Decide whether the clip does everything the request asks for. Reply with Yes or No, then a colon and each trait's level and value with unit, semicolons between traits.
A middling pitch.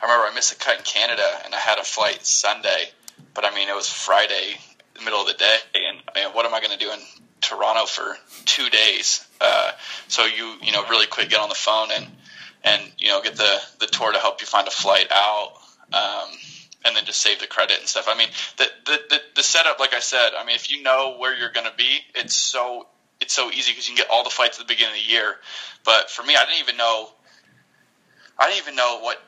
No: low, 120 Hz